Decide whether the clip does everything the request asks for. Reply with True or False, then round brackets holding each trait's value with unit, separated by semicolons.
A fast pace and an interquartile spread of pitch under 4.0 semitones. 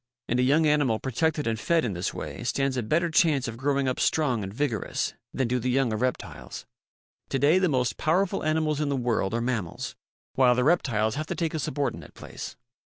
False (220 wpm; 4.7 semitones)